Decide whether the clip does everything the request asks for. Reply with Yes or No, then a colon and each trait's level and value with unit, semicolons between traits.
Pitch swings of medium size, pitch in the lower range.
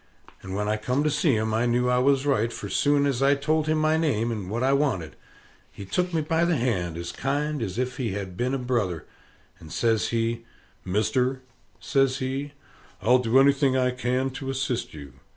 Yes: average, 4.1 semitones; low, 125 Hz